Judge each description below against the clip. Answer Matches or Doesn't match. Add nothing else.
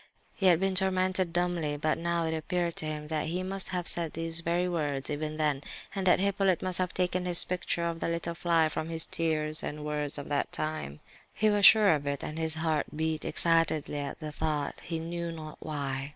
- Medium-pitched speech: Matches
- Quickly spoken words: Matches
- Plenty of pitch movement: Doesn't match